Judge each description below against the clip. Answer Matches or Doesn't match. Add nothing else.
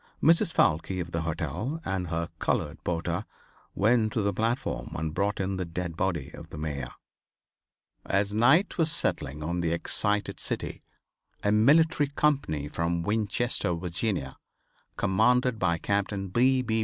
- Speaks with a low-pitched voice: Matches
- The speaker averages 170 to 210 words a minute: Doesn't match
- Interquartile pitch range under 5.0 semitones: Doesn't match